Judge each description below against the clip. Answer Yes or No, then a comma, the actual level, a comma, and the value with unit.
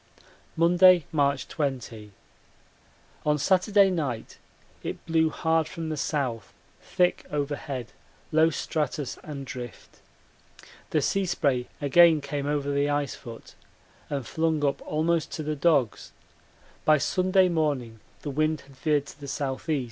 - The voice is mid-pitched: Yes, medium, 150 Hz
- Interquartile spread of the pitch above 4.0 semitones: No, average, 2.7 semitones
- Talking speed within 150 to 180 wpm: No, slow, 135 wpm